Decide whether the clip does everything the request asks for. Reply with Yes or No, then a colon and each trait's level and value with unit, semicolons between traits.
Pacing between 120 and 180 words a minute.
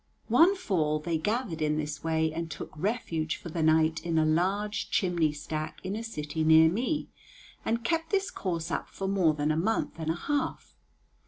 No: average, 190 wpm